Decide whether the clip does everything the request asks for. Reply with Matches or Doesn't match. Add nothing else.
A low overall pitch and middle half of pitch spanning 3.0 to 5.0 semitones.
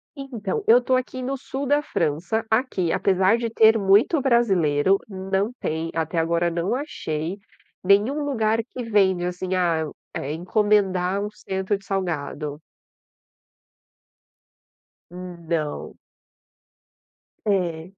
Doesn't match